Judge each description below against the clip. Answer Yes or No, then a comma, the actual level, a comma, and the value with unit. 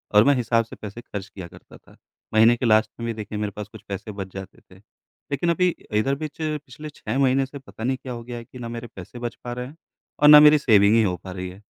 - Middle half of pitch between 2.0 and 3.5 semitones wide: No, average, 4.4 semitones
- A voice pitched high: No, low, 115 Hz